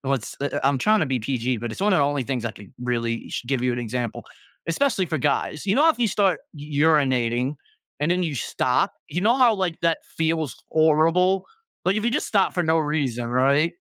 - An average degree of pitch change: No, wide, 6.2 semitones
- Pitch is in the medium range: Yes, medium, 150 Hz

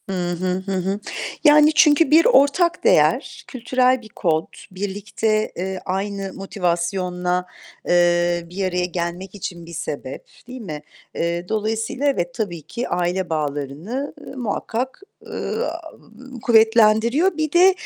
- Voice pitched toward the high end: Yes, high, 195 Hz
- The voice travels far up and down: Yes, wide, 6.0 semitones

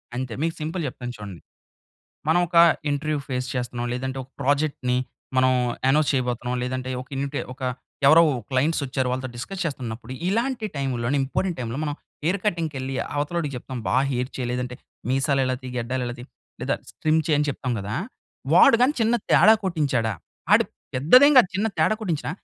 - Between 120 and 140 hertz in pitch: Yes, low, 135 Hz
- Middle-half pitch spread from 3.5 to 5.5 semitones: Yes, average, 4.2 semitones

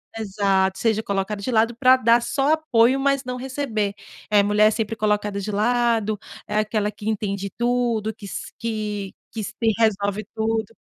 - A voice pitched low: No, high, 220 Hz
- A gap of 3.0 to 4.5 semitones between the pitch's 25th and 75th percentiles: No, narrow, 2.5 semitones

